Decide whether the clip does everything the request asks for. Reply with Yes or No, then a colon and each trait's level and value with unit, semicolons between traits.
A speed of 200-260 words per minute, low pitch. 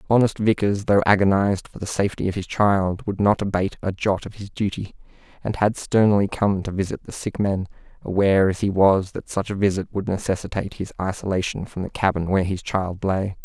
Yes: fast, 205 wpm; low, 100 Hz